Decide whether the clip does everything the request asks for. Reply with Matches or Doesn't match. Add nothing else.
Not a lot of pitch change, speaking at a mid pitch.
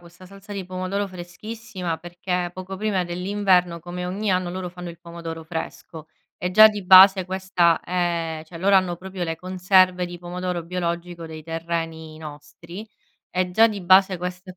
Matches